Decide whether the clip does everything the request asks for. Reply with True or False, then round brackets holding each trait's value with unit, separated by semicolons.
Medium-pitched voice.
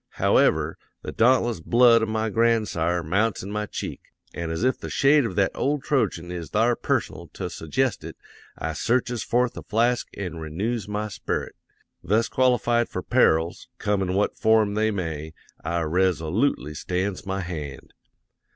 False (105 Hz)